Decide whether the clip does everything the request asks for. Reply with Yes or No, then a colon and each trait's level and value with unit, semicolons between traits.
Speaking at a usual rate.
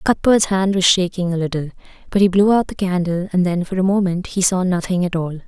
No: fast, 240 wpm